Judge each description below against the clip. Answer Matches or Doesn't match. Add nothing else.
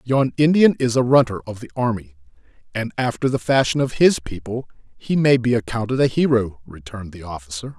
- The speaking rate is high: Doesn't match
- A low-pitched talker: Matches